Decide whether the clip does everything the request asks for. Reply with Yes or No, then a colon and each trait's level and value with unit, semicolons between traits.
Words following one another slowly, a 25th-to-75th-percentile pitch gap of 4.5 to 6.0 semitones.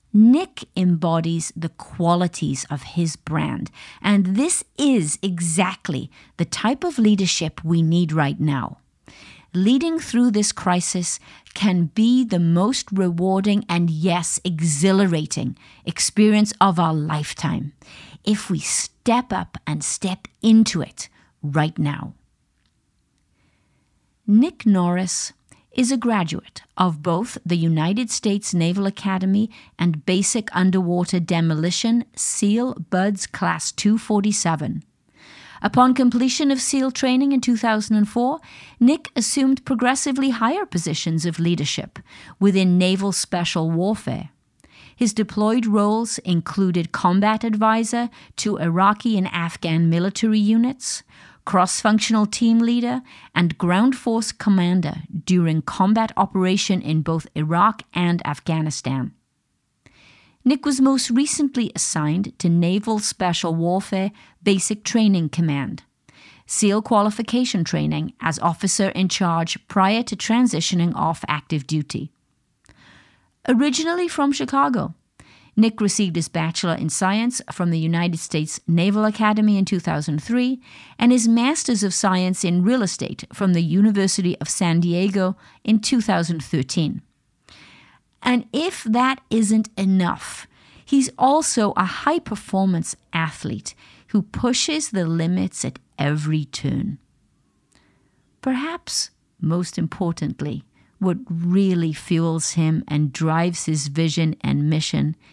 Yes: slow, 115 wpm; average, 5.1 semitones